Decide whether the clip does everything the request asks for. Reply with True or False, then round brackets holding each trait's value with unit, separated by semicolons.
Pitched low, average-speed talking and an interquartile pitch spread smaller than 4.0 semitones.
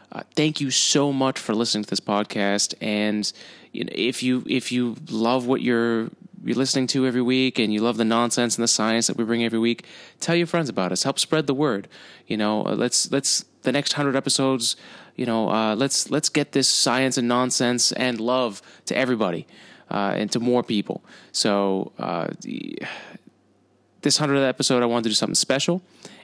True (125 Hz; 195 wpm; 3.4 semitones)